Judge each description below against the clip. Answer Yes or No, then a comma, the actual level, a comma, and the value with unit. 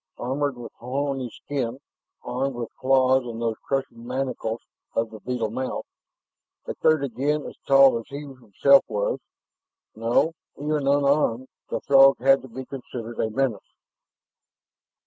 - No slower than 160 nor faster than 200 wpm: No, average, 140 wpm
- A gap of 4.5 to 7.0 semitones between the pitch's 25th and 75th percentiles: No, average, 2.8 semitones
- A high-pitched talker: No, low, 130 Hz